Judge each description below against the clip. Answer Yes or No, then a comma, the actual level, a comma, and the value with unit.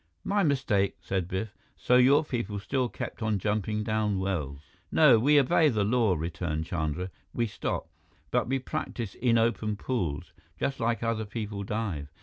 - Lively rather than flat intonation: No, average, 4.5 semitones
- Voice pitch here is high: No, low, 110 Hz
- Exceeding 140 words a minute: Yes, average, 160 wpm